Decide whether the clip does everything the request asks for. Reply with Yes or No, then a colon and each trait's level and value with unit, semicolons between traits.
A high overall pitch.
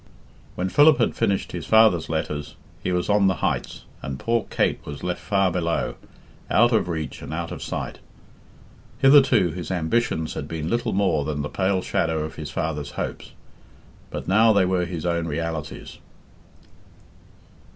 No: very low, 90 Hz